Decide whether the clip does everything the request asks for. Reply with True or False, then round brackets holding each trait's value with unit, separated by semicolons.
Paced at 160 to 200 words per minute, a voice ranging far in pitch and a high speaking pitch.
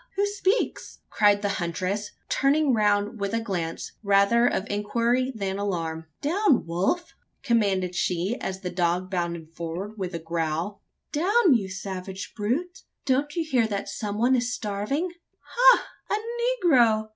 False (145 wpm; 6.2 semitones; 210 Hz)